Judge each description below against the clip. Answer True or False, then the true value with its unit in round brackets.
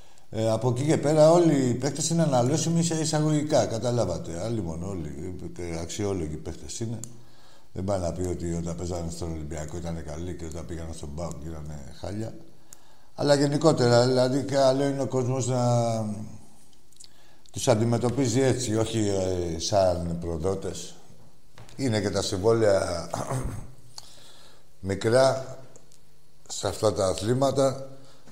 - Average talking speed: True (125 wpm)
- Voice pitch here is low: True (110 Hz)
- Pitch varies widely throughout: True (7.2 semitones)